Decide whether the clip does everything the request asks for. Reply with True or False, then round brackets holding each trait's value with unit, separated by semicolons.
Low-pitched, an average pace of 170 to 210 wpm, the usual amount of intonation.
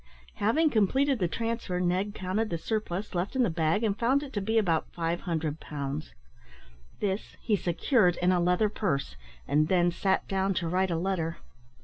False (185 Hz; 175 wpm; 4.1 semitones)